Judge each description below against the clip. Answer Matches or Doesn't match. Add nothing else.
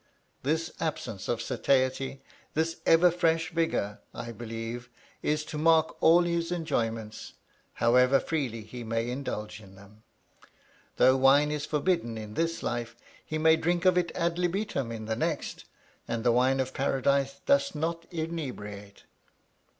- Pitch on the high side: Doesn't match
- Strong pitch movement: Matches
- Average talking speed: Matches